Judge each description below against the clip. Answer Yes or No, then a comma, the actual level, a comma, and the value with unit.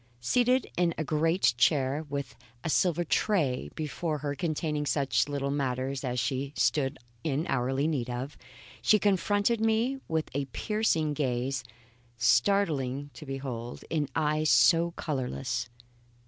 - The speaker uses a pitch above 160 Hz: No, medium, 145 Hz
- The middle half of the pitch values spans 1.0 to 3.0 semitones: No, average, 3.9 semitones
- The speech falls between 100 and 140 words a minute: Yes, slow, 135 wpm